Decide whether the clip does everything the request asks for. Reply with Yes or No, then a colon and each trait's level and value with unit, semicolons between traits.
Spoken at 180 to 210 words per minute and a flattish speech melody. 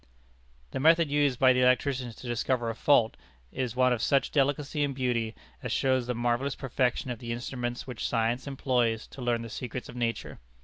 Yes: average, 190 wpm; narrow, 2.1 semitones